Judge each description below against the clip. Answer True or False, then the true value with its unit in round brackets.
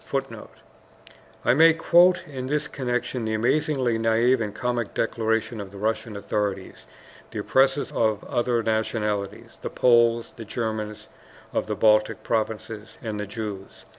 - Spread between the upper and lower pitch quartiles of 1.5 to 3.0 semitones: True (2.5 semitones)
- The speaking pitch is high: False (115 Hz)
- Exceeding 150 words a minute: False (140 wpm)